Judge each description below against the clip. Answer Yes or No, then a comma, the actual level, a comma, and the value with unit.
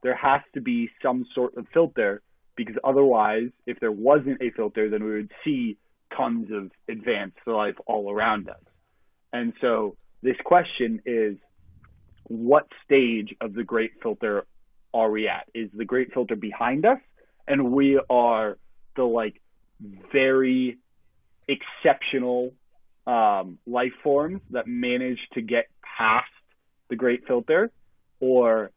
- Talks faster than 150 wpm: No, slow, 135 wpm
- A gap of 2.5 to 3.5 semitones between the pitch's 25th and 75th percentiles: Yes, average, 3.1 semitones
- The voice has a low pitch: Yes, low, 120 Hz